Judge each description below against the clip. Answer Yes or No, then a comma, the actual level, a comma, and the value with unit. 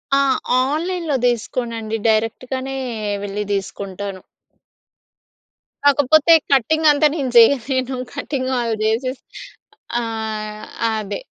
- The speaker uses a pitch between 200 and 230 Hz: No, very high, 255 Hz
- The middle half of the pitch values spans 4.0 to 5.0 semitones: Yes, average, 4.3 semitones